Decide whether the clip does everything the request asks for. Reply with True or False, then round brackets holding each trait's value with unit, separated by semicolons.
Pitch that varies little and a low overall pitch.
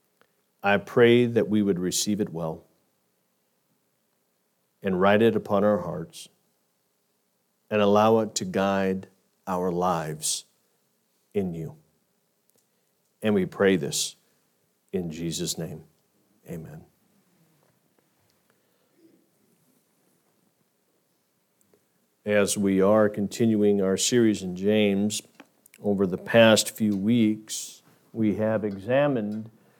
True (2.3 semitones; 105 Hz)